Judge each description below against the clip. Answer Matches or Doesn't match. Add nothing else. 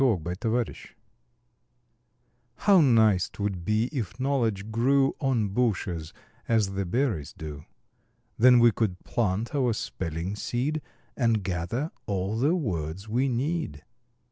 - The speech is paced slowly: Matches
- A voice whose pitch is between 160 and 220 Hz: Doesn't match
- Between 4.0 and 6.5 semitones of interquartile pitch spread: Matches